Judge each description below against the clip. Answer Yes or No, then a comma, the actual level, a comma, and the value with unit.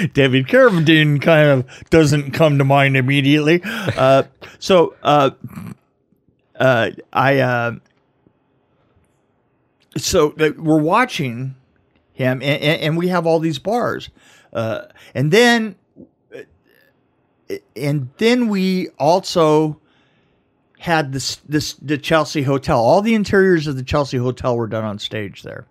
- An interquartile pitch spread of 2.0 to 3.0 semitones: No, average, 3.8 semitones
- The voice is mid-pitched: Yes, medium, 150 Hz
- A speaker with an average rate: No, slow, 120 wpm